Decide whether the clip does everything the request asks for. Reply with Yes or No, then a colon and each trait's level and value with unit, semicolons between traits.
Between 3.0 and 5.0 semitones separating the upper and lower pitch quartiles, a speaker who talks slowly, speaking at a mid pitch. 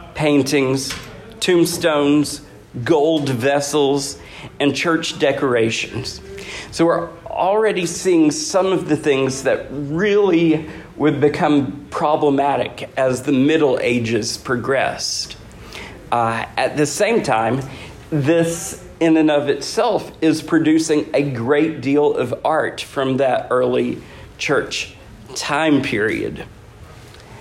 Yes: average, 3.3 semitones; slow, 105 wpm; medium, 145 Hz